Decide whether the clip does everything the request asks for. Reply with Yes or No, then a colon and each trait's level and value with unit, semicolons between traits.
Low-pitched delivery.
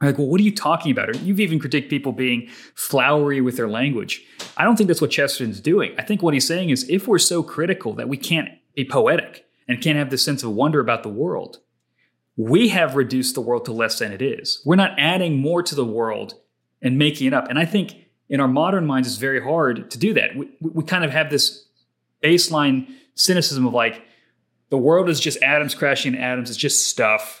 No: medium, 145 Hz